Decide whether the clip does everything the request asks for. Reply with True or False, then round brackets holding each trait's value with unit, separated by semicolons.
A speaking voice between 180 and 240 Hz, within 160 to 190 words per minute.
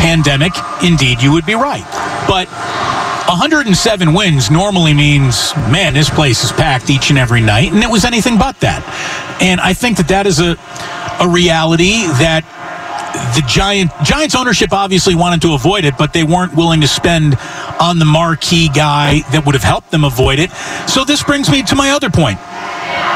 False (165 Hz; 180 wpm)